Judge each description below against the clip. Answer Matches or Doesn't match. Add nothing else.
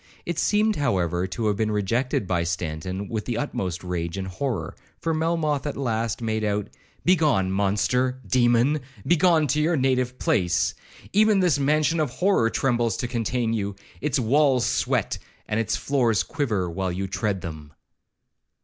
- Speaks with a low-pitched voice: Matches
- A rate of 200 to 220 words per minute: Doesn't match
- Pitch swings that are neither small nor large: Doesn't match